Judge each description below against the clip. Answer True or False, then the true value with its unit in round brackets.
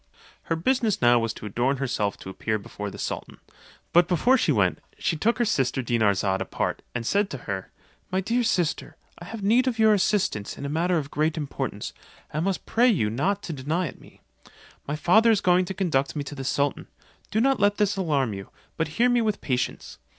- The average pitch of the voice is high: False (165 Hz)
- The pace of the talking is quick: True (210 wpm)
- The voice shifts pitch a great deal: True (7.9 semitones)